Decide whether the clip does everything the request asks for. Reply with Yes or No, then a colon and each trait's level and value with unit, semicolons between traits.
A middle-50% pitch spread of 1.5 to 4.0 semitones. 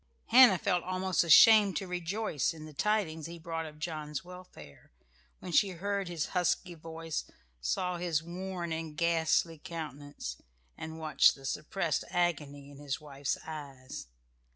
Yes: average, 3.1 semitones